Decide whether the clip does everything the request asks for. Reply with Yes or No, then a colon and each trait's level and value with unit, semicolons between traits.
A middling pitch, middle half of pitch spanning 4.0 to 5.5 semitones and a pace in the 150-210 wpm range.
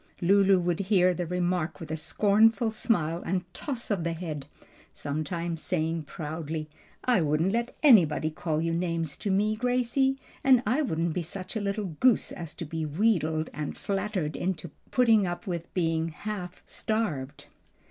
Yes: medium, 175 Hz; average, 4.7 semitones; average, 160 wpm